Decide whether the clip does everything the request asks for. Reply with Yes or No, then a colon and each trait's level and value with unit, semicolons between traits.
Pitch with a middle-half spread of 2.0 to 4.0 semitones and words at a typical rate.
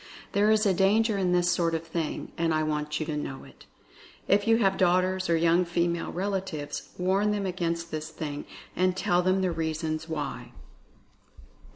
Yes: average, 3.1 semitones; average, 180 wpm